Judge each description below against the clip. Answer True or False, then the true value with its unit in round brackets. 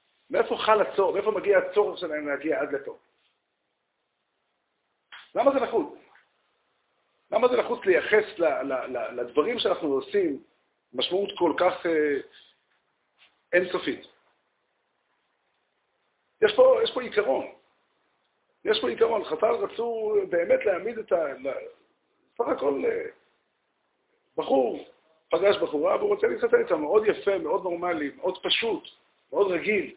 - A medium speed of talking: True (110 wpm)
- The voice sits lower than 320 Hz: False (370 Hz)